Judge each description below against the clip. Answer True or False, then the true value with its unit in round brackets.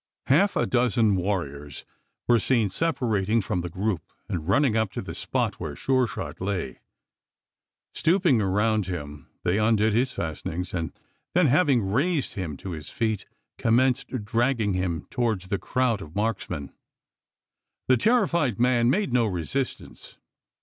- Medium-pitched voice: False (110 Hz)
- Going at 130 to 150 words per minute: True (145 wpm)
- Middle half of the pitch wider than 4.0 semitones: True (5.5 semitones)